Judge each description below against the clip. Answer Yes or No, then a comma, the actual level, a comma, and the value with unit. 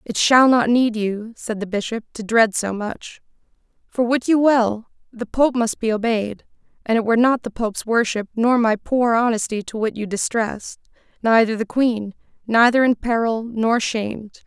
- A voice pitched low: No, high, 225 Hz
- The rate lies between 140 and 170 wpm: No, average, 180 wpm